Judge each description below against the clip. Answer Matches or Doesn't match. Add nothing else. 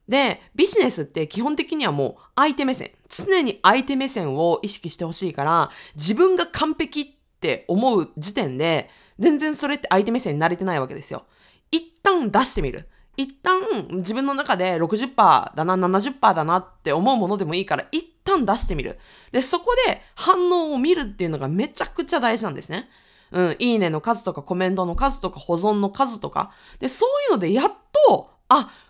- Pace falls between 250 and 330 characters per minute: Doesn't match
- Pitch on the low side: Doesn't match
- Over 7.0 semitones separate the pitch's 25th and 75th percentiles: Matches